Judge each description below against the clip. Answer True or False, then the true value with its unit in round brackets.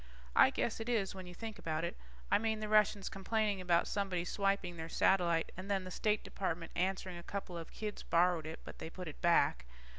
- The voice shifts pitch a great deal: False (3.0 semitones)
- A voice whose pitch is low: False (185 Hz)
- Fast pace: True (215 wpm)